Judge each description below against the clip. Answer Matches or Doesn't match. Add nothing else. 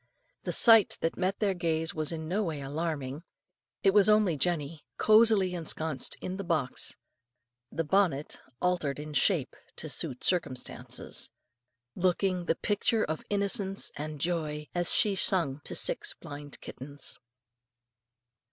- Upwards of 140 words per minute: Doesn't match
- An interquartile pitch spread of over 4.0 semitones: Matches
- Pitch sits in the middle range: Matches